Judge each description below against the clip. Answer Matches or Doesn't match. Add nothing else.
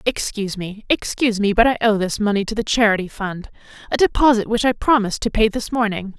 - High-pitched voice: Matches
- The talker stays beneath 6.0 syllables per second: Doesn't match